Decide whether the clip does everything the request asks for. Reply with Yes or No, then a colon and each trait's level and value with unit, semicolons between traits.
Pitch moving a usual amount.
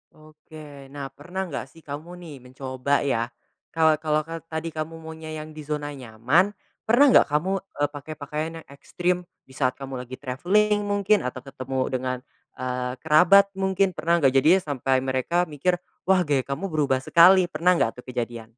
Yes: average, 4.5 semitones